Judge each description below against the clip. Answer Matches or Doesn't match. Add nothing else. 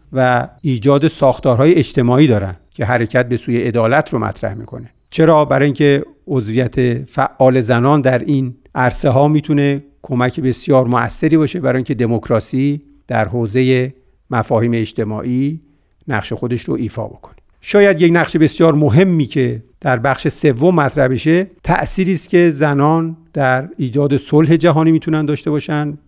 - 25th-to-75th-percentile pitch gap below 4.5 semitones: Matches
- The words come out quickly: Doesn't match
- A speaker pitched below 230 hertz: Matches